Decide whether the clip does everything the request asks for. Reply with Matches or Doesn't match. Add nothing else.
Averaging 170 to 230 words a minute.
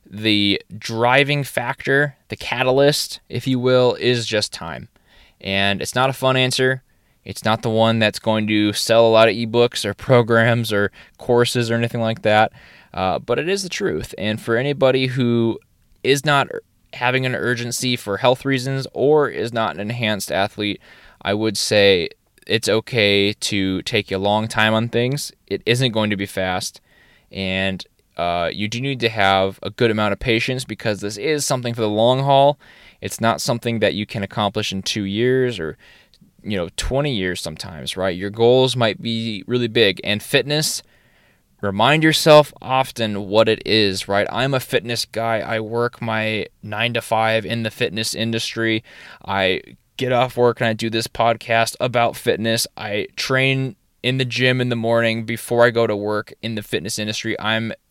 Matches